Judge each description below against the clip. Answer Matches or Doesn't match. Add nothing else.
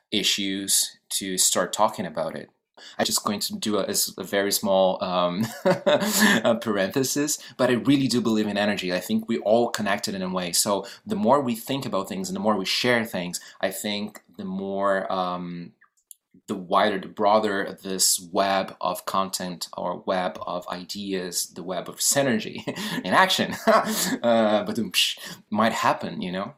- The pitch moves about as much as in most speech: Matches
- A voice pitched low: Matches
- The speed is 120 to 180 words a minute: Matches